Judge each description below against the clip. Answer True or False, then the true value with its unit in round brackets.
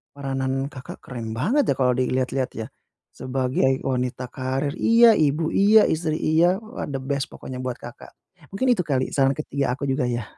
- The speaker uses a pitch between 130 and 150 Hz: True (135 Hz)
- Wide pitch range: False (3.5 semitones)